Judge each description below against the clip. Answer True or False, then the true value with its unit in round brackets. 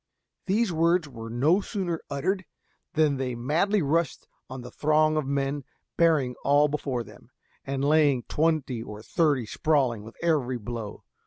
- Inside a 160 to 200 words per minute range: False (150 wpm)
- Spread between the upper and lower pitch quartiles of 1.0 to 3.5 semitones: False (4.4 semitones)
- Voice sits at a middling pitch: True (145 Hz)